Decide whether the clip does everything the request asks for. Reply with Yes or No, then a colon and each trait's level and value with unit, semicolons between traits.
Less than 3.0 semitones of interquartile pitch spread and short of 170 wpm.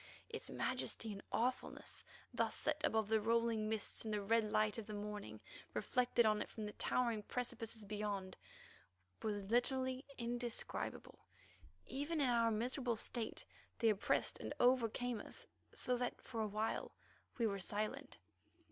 Yes: narrow, 2.6 semitones; average, 145 wpm